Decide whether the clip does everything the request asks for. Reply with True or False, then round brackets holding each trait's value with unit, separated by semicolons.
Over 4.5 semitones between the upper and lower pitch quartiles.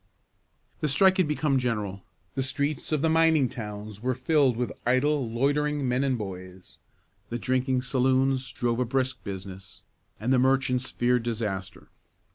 False (3.2 semitones)